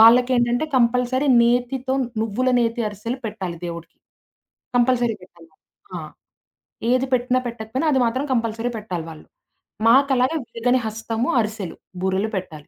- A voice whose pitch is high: Yes, high, 235 Hz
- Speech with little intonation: No, average, 3.0 semitones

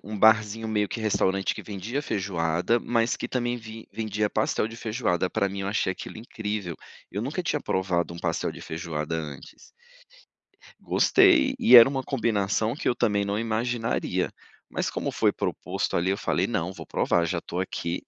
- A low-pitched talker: Yes, low, 105 Hz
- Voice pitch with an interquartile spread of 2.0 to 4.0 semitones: Yes, average, 3.7 semitones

